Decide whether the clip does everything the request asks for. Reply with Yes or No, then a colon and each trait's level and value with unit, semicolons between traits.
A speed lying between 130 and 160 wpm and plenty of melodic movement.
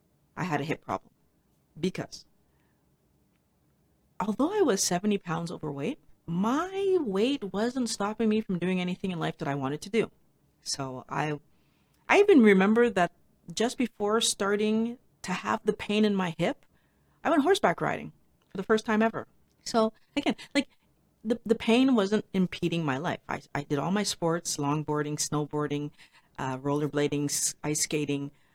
Yes: average, 155 wpm; wide, 6.9 semitones